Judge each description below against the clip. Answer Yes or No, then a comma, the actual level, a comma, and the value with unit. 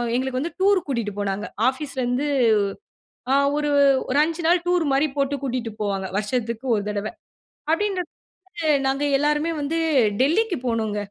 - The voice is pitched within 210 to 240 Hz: No, very high, 270 Hz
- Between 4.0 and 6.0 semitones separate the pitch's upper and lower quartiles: Yes, wide, 5.4 semitones